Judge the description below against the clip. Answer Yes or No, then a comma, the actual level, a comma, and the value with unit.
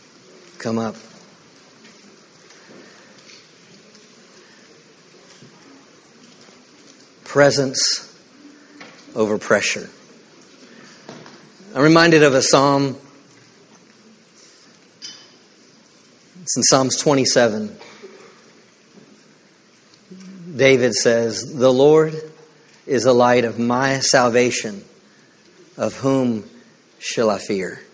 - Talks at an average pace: No, slow, 60 wpm